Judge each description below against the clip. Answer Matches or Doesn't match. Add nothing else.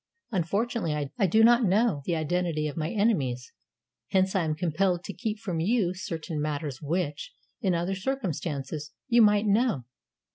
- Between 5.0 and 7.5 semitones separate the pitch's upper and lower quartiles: Matches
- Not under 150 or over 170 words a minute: Matches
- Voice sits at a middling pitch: Matches